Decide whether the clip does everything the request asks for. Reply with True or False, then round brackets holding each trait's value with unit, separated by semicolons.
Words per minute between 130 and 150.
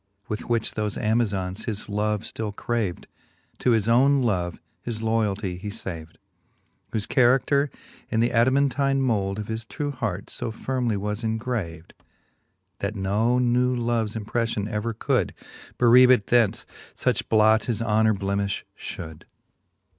True (140 wpm)